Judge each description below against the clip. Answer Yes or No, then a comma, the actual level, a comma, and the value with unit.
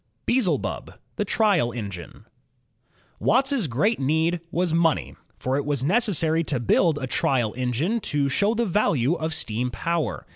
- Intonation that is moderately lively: No, wide, 6.8 semitones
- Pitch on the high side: No, medium, 160 Hz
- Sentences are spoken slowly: No, average, 145 wpm